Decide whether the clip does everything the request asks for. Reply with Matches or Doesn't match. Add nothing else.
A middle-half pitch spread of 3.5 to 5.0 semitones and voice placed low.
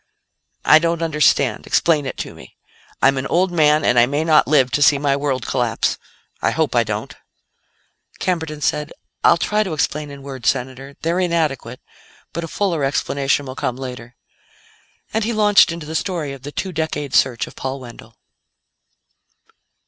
Doesn't match